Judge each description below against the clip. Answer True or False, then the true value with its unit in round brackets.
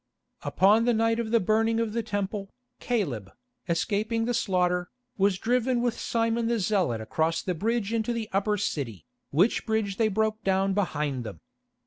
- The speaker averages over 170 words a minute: False (165 wpm)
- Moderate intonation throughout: True (3.9 semitones)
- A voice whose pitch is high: True (210 Hz)